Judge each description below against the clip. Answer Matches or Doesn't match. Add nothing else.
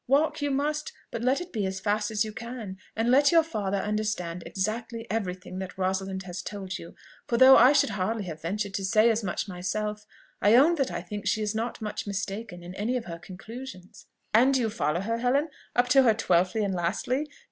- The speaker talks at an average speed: Doesn't match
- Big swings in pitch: Doesn't match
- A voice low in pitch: Doesn't match